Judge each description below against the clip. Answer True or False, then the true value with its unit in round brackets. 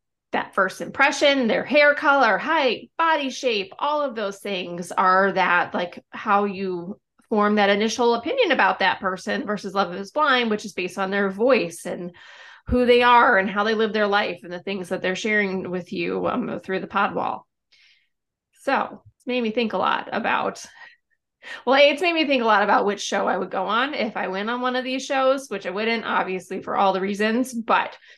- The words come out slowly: False (205 wpm)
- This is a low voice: False (210 Hz)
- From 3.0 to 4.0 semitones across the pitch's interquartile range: False (5.0 semitones)